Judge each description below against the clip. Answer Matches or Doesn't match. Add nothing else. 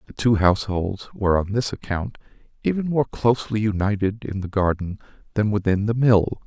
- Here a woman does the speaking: Doesn't match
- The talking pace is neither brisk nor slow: Matches